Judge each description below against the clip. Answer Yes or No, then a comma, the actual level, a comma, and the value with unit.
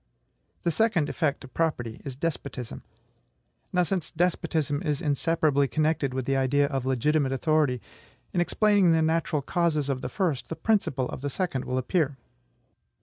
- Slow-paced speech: No, average, 155 wpm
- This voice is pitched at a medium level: Yes, medium, 150 Hz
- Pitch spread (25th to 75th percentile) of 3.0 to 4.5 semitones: Yes, average, 3.8 semitones